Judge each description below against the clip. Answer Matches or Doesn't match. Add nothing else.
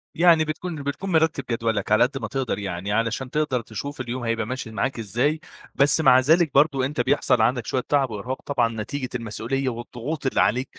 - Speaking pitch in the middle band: Doesn't match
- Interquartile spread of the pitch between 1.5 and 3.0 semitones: Doesn't match